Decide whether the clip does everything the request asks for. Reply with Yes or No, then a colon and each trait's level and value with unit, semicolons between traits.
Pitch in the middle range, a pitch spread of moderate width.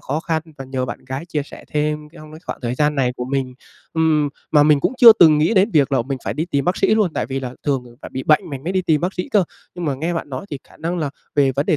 Yes: medium, 150 Hz; average, 3.5 semitones